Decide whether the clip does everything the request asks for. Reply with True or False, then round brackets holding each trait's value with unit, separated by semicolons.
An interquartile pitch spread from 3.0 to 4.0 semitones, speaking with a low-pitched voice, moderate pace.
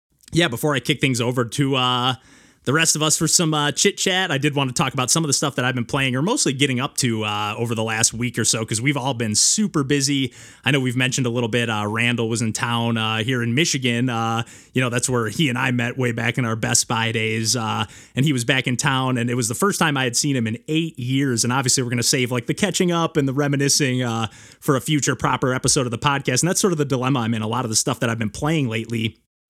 False (3.7 semitones; 130 Hz; 285 wpm)